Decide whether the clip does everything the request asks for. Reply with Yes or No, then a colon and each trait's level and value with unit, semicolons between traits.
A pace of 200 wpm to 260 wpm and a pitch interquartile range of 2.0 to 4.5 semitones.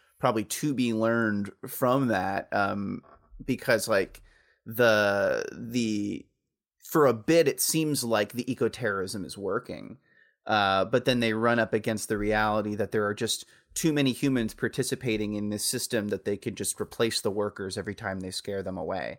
No: average, 170 wpm; average, 3.2 semitones